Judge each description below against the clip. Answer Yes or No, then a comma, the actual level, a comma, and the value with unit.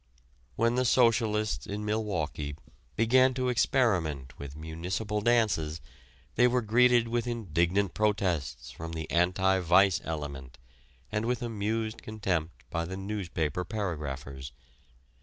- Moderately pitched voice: No, low, 100 Hz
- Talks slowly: Yes, slow, 120 wpm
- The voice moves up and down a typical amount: No, wide, 5.9 semitones